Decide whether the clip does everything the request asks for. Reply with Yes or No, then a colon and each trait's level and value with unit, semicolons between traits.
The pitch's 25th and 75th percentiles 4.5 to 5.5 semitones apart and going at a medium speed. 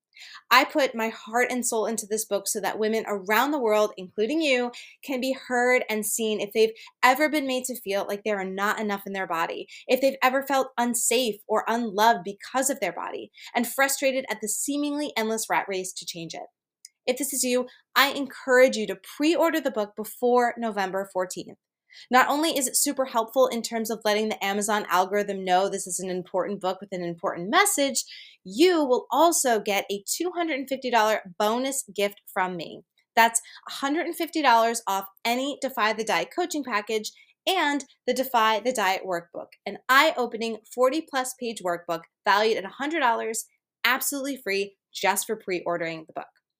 Yes: average, 4.8 semitones; average, 180 wpm